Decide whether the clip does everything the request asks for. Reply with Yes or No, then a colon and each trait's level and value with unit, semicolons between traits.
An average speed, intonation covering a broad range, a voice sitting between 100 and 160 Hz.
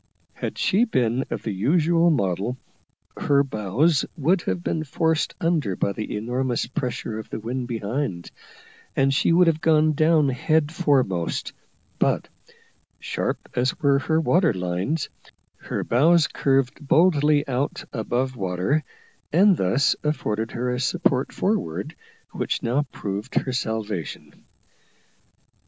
No: slow, 130 wpm; wide, 5.9 semitones; low, 135 Hz